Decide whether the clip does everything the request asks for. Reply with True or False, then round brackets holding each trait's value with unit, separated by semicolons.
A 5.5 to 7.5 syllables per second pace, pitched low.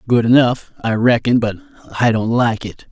False (5.0 syllables/s; 125 Hz)